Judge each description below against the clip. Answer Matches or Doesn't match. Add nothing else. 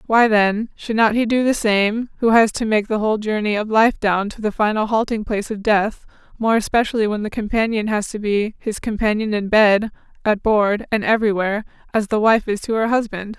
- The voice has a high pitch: Matches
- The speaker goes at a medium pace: Doesn't match